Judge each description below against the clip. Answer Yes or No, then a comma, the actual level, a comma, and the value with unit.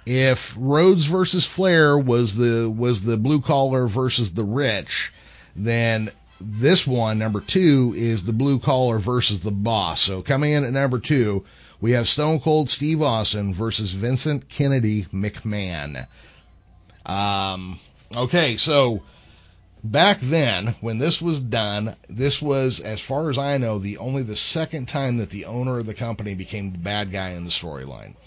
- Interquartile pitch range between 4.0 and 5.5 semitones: Yes, average, 5.2 semitones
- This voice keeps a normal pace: Yes, average, 160 wpm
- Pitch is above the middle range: No, low, 115 Hz